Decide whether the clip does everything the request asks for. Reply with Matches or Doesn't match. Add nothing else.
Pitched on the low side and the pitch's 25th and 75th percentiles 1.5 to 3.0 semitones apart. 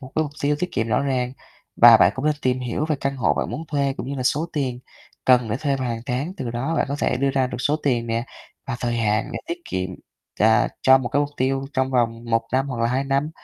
Matches